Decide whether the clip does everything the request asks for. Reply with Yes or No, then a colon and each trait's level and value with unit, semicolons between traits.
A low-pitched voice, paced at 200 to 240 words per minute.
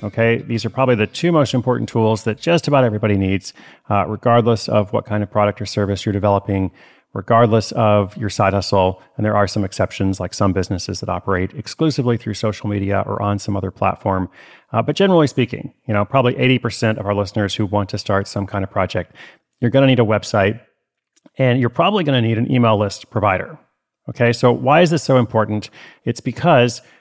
Yes: low, 110 Hz; fast, 205 wpm